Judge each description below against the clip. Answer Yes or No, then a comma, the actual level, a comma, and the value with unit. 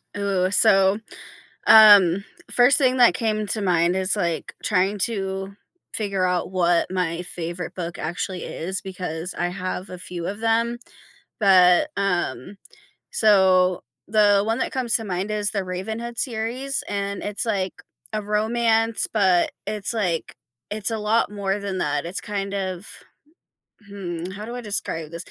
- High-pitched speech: Yes, high, 195 Hz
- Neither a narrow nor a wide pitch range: Yes, average, 3.0 semitones